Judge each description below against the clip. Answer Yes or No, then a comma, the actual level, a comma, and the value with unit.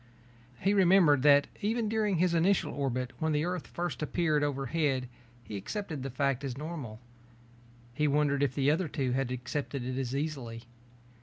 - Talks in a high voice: No, medium, 145 Hz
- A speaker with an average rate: Yes, average, 165 wpm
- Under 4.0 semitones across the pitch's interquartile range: No, average, 4.4 semitones